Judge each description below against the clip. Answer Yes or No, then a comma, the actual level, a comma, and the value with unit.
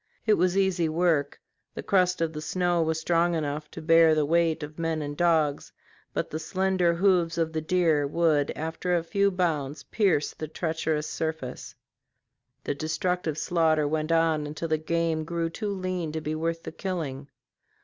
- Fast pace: No, average, 175 wpm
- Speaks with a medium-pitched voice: Yes, medium, 165 Hz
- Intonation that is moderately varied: No, narrow, 2.0 semitones